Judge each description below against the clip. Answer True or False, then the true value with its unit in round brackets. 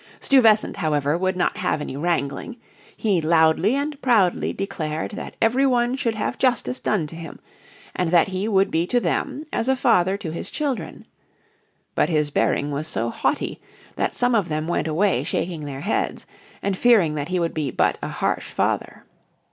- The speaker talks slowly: False (180 wpm)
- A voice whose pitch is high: False (180 Hz)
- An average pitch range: False (6.4 semitones)